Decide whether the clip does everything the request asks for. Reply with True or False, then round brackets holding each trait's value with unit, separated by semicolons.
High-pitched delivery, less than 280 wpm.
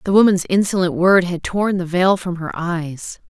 False (180 Hz; 200 wpm)